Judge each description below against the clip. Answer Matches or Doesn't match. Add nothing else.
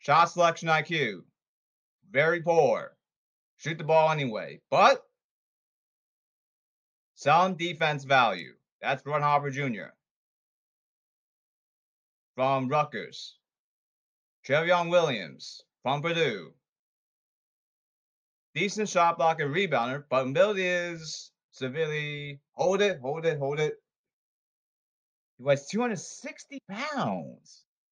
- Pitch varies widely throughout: Doesn't match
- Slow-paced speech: Matches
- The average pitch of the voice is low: Doesn't match